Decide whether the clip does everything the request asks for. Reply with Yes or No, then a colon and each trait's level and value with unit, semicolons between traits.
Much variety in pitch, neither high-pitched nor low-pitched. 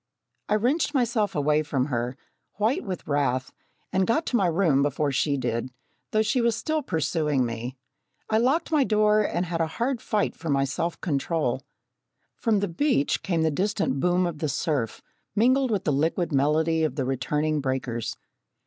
Yes: wide, 7.1 semitones; medium, 165 Hz